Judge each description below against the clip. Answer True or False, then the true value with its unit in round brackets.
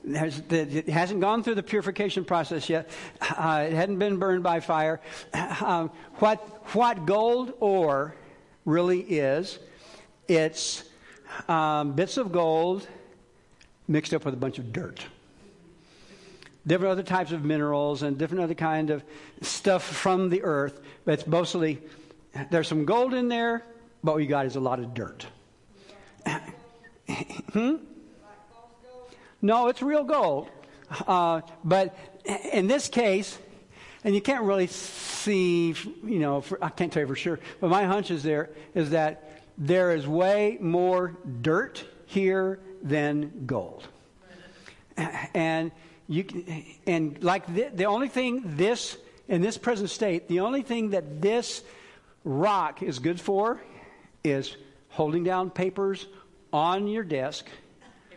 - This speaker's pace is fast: False (140 wpm)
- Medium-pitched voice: True (175 Hz)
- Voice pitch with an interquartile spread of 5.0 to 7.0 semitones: False (4.3 semitones)